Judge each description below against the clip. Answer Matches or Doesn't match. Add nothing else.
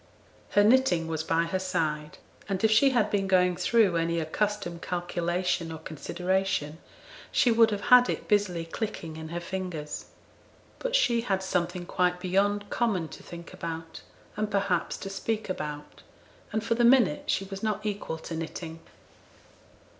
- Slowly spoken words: Doesn't match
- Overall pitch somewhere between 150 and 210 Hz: Matches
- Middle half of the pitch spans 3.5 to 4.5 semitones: Matches